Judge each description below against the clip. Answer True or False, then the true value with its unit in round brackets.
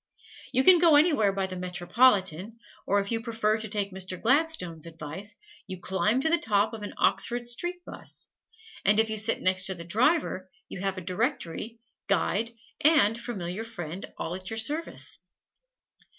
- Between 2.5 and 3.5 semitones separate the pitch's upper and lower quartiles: False (4.3 semitones)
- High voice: True (210 Hz)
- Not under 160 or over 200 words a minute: True (165 wpm)